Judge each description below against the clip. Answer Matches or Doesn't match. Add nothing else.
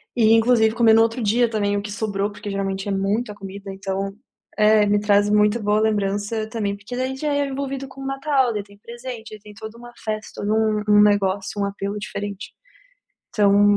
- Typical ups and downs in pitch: Doesn't match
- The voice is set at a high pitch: Matches